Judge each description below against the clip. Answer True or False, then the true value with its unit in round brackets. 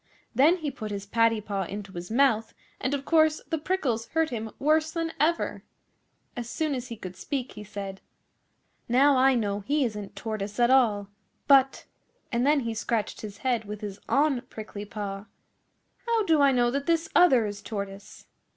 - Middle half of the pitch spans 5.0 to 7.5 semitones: True (5.3 semitones)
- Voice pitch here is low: False (240 Hz)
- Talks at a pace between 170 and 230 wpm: True (180 wpm)